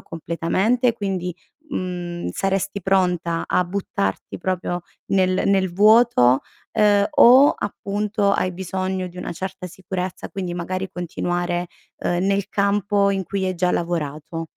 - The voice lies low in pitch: No, medium, 185 Hz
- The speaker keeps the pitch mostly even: Yes, narrow, 2.2 semitones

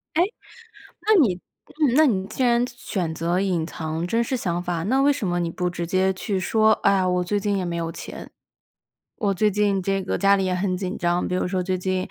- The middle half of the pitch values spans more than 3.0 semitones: No, narrow, 2.6 semitones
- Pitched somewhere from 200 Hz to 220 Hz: No, medium, 185 Hz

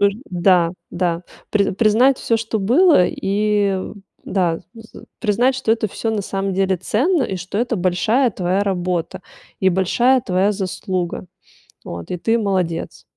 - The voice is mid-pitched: No, high, 195 Hz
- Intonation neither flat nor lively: Yes, average, 3.6 semitones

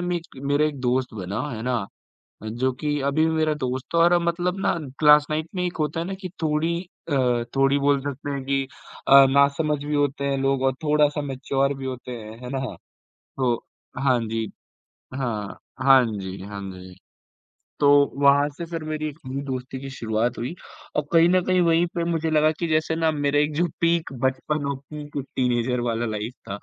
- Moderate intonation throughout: Yes, average, 3.5 semitones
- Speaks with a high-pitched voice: No, medium, 140 Hz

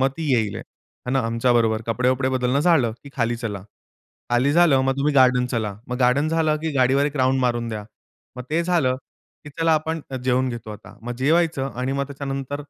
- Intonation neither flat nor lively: Yes, average, 3.0 semitones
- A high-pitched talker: No, low, 130 Hz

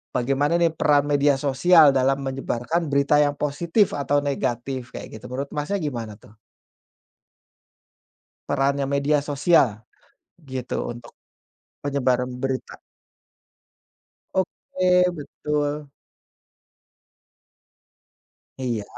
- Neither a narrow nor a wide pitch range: No, narrow, 2.3 semitones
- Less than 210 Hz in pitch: Yes, medium, 140 Hz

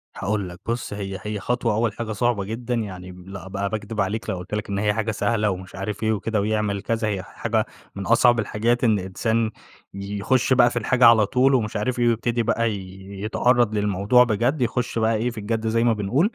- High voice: No, low, 110 Hz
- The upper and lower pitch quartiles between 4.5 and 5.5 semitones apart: No, average, 2.7 semitones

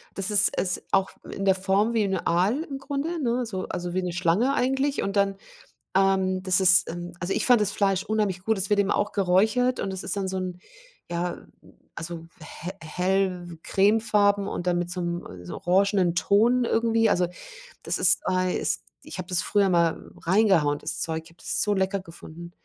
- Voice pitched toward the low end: No, high, 190 Hz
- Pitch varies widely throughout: No, average, 2.8 semitones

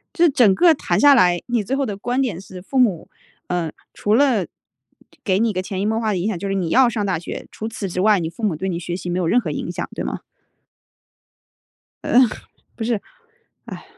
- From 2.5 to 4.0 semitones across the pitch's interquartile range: No, average, 5.0 semitones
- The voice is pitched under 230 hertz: Yes, high, 200 Hz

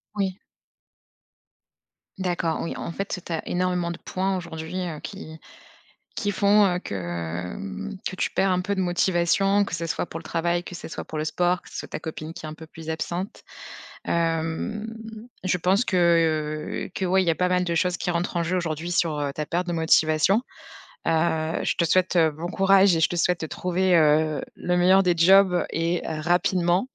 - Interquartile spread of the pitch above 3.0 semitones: No, narrow, 2.4 semitones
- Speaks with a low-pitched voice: No, medium, 175 Hz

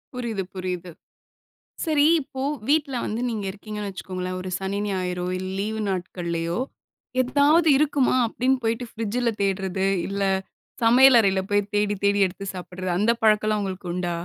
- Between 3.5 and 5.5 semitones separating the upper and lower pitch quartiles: Yes, average, 4.1 semitones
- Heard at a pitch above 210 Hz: No, high, 205 Hz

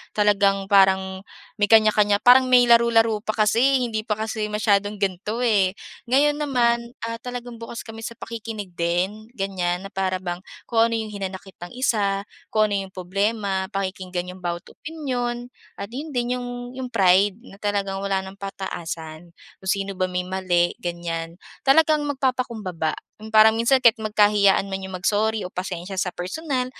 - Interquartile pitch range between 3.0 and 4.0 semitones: Yes, average, 3.7 semitones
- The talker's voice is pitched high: Yes, high, 205 Hz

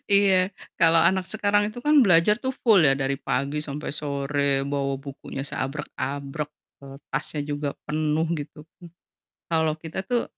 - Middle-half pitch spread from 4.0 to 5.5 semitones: Yes, average, 4.9 semitones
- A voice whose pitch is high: No, medium, 150 Hz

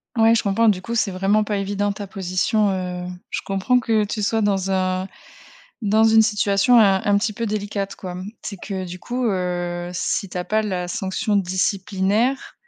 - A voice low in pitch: No, high, 200 Hz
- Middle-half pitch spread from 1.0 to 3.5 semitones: Yes, narrow, 2.5 semitones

